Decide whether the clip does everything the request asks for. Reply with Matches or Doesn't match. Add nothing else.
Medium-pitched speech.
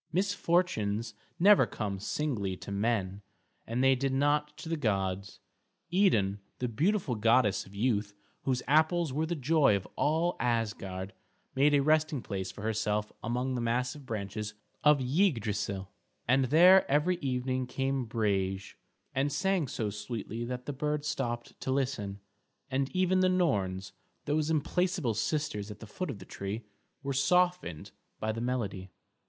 Doesn't match